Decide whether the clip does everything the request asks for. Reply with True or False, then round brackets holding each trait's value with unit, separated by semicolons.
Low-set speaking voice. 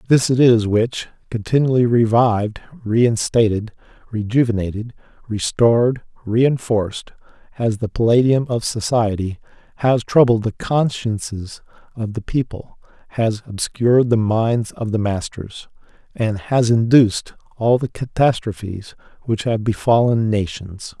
True (115 Hz)